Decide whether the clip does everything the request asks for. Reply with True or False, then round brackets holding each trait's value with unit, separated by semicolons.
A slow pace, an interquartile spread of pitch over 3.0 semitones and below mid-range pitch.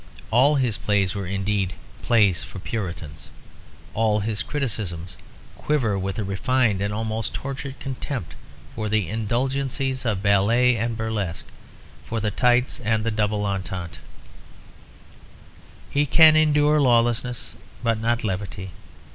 True (125 wpm; 3.9 semitones; 110 Hz)